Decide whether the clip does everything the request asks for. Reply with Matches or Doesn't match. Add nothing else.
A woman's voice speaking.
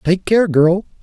Doesn't match